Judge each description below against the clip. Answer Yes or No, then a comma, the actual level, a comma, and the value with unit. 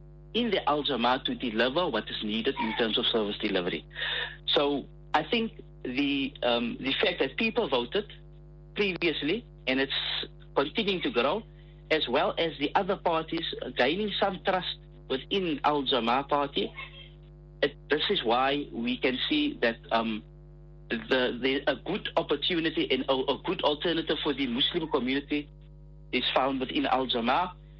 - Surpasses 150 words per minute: No, average, 145 wpm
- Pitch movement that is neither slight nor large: Yes, average, 4.1 semitones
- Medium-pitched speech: Yes, medium, 160 Hz